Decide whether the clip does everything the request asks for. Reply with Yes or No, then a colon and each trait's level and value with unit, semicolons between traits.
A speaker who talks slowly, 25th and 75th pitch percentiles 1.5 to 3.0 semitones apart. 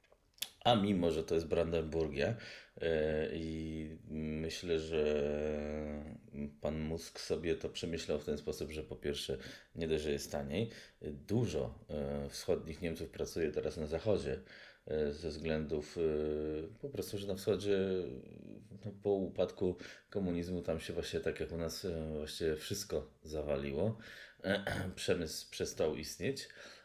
No: average, 120 wpm; narrow, 2.5 semitones